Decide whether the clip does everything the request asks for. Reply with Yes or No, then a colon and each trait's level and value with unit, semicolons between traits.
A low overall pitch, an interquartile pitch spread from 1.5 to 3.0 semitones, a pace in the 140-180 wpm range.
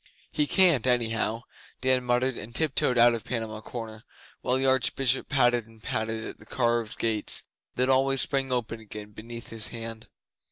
Yes: low, 120 Hz; narrow, 2.6 semitones; average, 165 wpm